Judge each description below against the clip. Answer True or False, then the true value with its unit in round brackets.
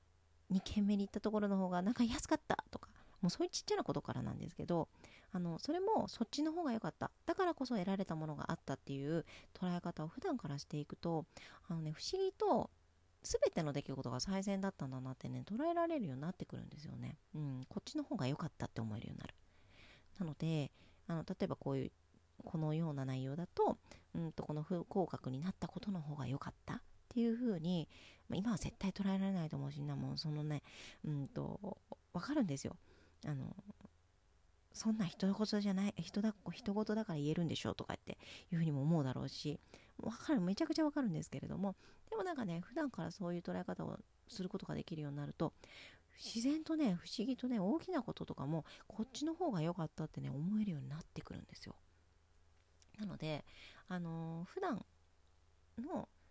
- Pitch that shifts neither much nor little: False (7.3 semitones)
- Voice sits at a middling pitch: True (170 Hz)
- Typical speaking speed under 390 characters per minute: False (410 characters per minute)